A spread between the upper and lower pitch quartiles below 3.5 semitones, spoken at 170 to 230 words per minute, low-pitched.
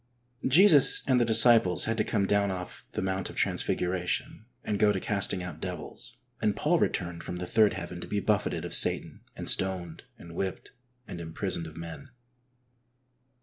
No: average, 3.9 semitones; average, 175 wpm; very low, 95 Hz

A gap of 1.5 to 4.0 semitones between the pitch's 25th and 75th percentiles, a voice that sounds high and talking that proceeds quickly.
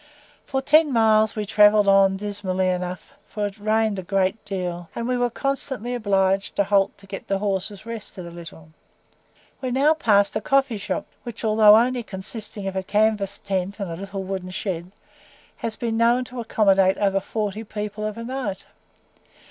No: average, 2.8 semitones; high, 205 Hz; average, 175 wpm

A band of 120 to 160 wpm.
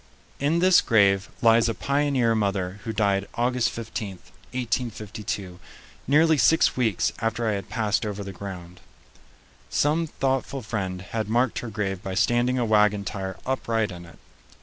Yes: average, 150 wpm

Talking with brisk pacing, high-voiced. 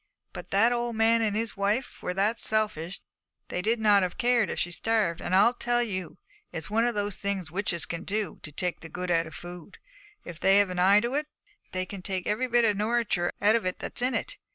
Yes: fast, 225 wpm; high, 205 Hz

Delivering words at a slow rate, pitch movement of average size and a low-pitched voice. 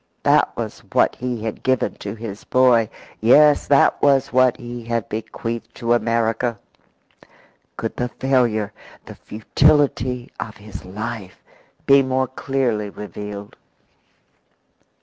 Yes: slow, 120 wpm; average, 3.0 semitones; low, 120 Hz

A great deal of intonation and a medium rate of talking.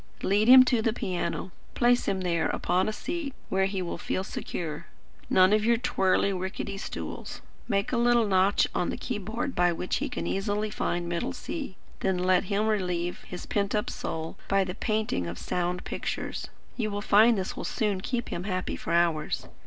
No: average, 3.2 semitones; average, 190 wpm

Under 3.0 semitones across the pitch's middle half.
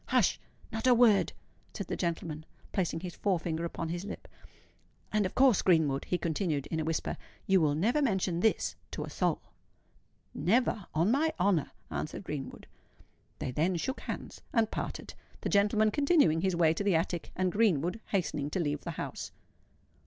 No: average, 4.7 semitones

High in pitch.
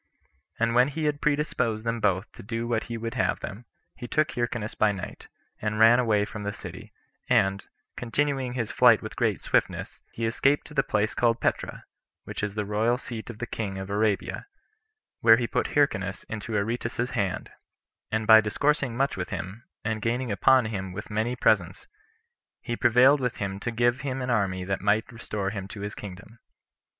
No: low, 115 Hz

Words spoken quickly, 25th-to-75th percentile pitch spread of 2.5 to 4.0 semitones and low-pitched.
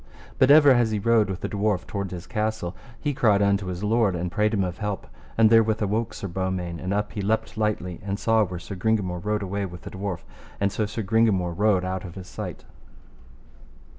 Yes: fast, 220 wpm; average, 2.9 semitones; low, 100 Hz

